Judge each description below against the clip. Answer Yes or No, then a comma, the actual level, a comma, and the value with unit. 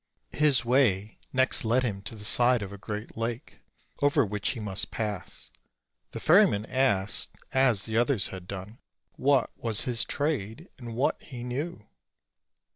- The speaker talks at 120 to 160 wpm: Yes, average, 155 wpm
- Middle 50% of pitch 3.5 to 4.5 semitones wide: Yes, average, 4.2 semitones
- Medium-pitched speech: No, low, 115 Hz